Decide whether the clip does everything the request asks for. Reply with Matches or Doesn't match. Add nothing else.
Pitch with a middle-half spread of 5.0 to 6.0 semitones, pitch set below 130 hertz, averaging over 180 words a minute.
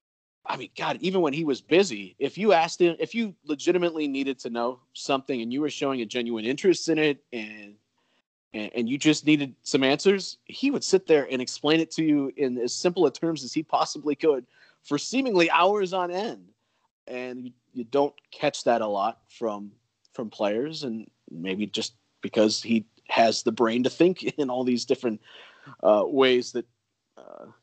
Doesn't match